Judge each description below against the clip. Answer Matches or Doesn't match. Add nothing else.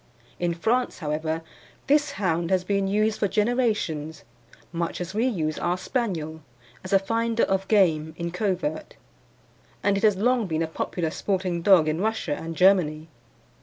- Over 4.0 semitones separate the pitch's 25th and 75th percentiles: Matches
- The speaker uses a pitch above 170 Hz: Matches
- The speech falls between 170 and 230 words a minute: Doesn't match